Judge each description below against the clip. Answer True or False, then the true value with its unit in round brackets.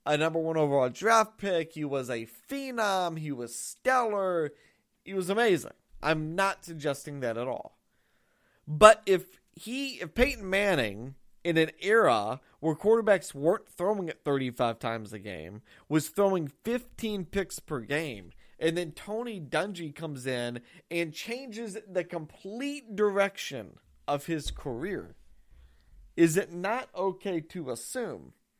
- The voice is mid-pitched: True (170 Hz)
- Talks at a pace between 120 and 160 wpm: True (140 wpm)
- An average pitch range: False (6.0 semitones)